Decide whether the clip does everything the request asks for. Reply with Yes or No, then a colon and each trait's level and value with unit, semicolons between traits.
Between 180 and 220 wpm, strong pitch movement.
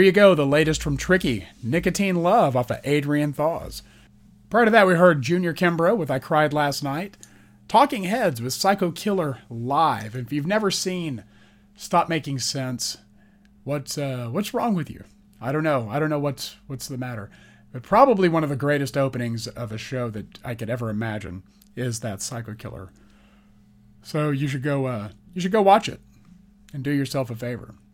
Yes: average, 190 wpm; wide, 6.7 semitones